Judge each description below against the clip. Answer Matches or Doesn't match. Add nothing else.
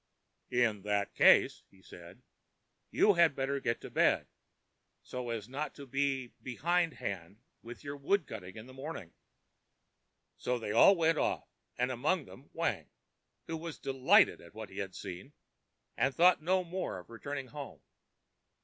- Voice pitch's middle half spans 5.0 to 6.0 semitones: Matches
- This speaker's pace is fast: Doesn't match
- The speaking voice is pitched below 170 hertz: Matches